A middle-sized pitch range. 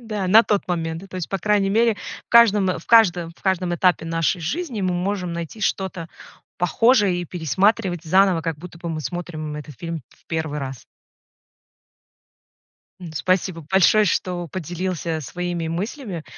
Yes: average, 3.0 semitones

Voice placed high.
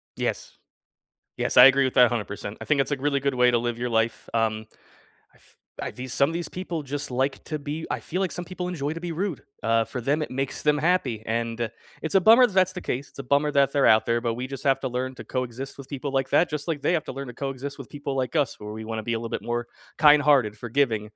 No: low, 135 Hz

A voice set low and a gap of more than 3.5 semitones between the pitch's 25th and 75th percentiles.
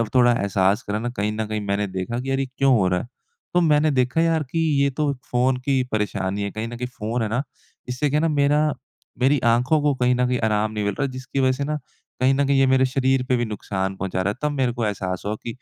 Yes: low, 125 Hz; average, 4.4 semitones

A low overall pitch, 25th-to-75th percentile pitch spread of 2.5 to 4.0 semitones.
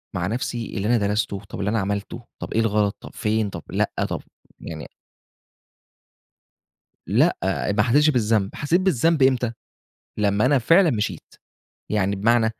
Yes: low, 110 Hz; average, 3.5 semitones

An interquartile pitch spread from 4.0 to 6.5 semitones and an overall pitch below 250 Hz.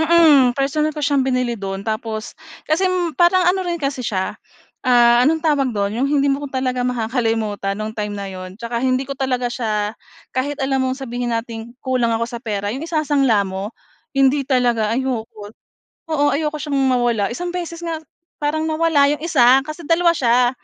No: average, 4.4 semitones; very high, 255 Hz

